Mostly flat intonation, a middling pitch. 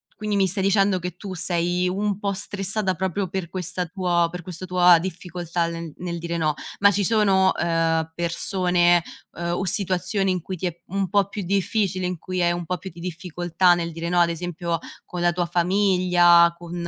Yes: narrow, 1.8 semitones; medium, 180 Hz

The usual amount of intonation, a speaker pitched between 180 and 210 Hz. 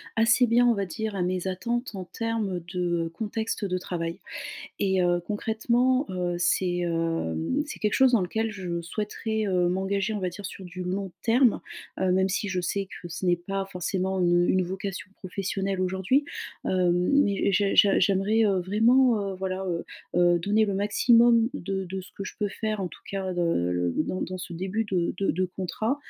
Yes: average, 3.2 semitones; high, 190 Hz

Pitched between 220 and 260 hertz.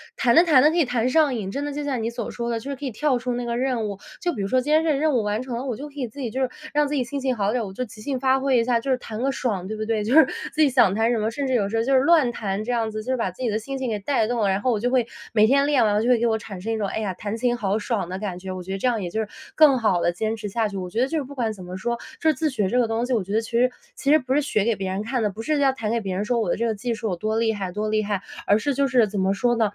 Yes: high, 235 Hz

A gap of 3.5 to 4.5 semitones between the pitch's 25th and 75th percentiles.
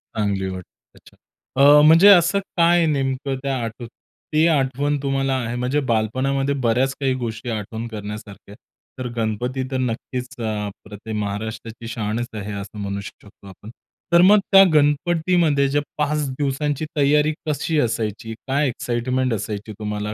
No: average, 4.9 semitones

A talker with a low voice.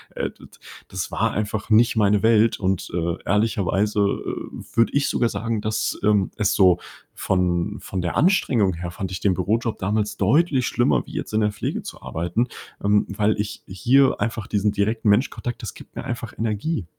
Yes: low, 105 Hz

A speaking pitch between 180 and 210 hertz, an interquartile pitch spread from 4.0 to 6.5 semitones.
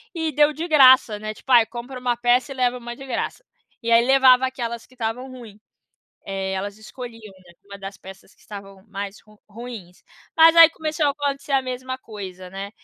No: high, 240 Hz; average, 4.4 semitones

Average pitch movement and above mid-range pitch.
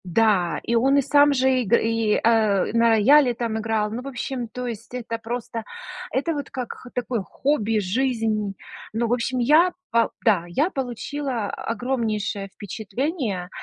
Yes: average, 3.2 semitones; high, 230 Hz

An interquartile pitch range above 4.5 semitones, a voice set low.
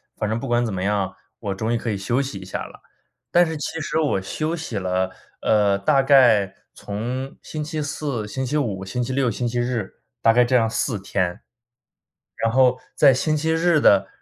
Yes: average, 5.3 semitones; low, 120 Hz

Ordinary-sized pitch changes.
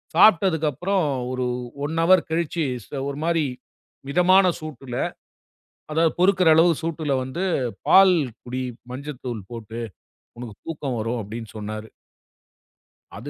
No: wide, 5.7 semitones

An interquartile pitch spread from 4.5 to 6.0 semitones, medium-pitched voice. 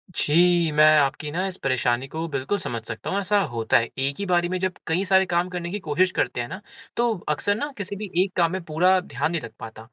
Yes: wide, 5.4 semitones; medium, 170 Hz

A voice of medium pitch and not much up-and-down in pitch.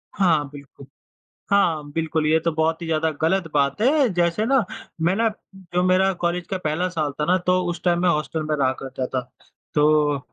No: medium, 165 Hz; average, 3.3 semitones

